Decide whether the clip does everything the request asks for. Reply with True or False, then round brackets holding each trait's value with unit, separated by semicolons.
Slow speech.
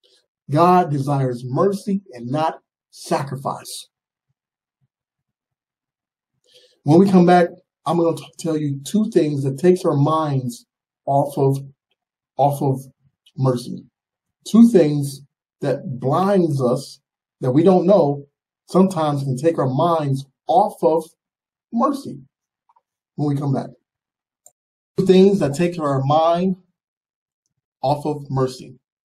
True (115 wpm)